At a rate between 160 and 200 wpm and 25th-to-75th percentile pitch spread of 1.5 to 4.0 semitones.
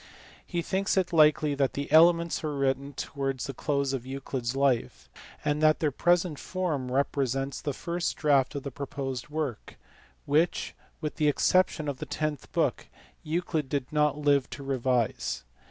Yes: average, 165 wpm; narrow, 2.5 semitones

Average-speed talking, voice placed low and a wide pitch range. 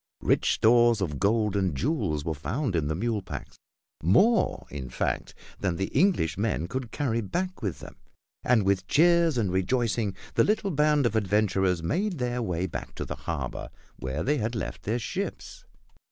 Yes: average, 175 wpm; low, 110 Hz; wide, 6.6 semitones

